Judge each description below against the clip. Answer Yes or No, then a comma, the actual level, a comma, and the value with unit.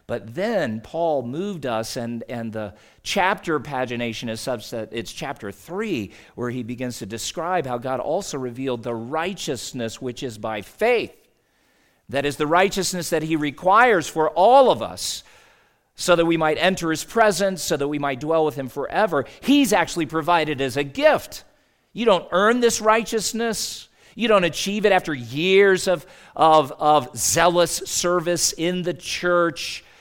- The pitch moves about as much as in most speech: No, wide, 6.4 semitones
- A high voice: No, medium, 160 Hz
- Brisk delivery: No, average, 160 wpm